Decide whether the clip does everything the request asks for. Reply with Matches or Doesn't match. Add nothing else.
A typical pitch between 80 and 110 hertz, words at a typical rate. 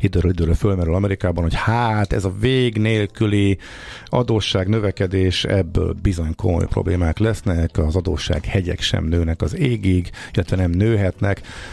Matches